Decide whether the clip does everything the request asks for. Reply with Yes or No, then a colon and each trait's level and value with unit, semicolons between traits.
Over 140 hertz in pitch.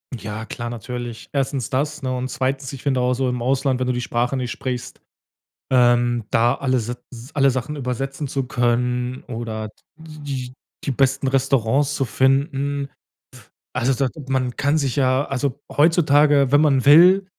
No: low, 130 Hz